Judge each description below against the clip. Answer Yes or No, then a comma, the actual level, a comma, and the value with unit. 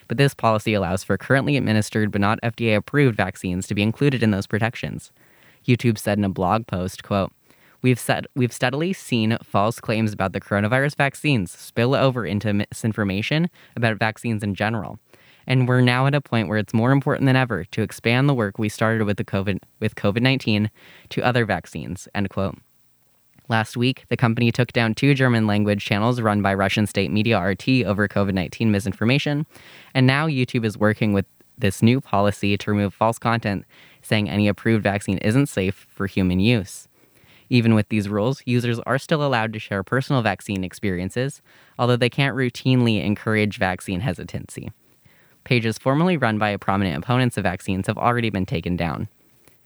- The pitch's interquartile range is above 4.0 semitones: No, average, 3.6 semitones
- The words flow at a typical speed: Yes, average, 175 wpm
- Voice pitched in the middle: No, low, 110 Hz